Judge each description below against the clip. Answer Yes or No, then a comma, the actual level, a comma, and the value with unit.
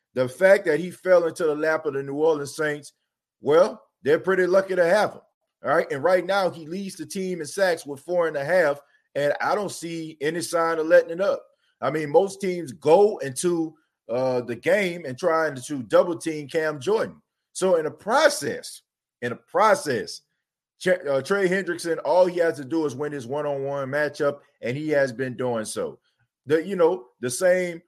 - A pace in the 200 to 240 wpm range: Yes, fast, 205 wpm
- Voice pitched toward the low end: No, medium, 165 Hz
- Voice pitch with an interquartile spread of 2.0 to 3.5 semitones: No, average, 4.2 semitones